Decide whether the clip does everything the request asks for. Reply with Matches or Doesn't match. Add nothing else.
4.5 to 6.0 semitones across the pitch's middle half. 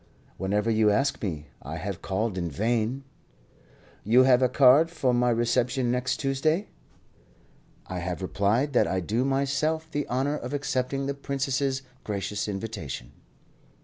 Matches